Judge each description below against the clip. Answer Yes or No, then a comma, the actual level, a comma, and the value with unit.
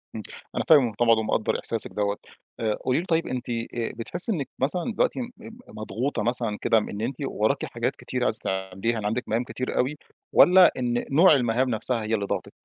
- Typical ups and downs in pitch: Yes, average, 3.5 semitones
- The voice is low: Yes, low, 120 Hz